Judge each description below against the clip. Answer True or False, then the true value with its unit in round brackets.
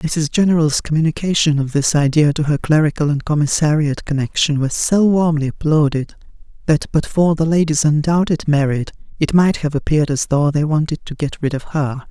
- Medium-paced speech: True (180 wpm)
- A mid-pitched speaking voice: True (150 Hz)